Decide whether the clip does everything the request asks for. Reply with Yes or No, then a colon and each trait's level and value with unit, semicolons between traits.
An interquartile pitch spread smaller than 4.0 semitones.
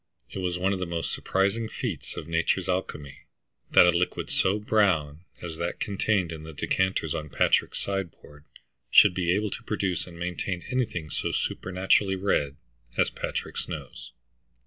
Yes: average, 2.8 semitones